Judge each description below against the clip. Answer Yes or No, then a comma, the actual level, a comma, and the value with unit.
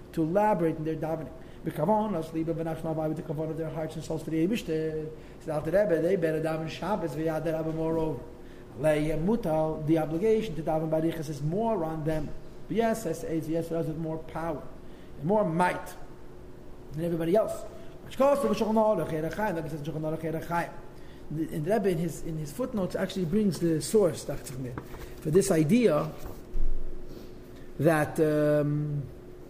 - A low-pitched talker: No, medium, 160 Hz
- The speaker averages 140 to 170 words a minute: Yes, average, 150 wpm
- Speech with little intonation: Yes, narrow, 1.5 semitones